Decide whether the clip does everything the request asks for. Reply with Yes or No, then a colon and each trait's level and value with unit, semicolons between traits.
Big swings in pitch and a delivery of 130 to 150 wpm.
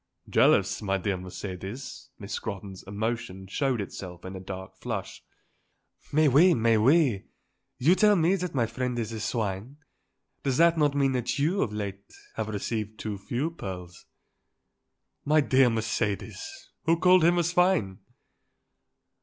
Yes: wide, 7.5 semitones; average, 145 wpm